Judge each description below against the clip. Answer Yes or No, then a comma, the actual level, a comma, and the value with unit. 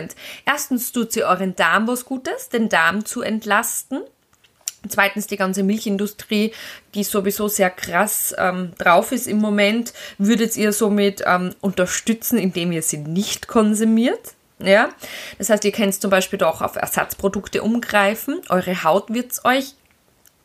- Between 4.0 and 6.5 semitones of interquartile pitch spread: No, average, 2.9 semitones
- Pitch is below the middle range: No, high, 205 Hz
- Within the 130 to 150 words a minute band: Yes, average, 145 wpm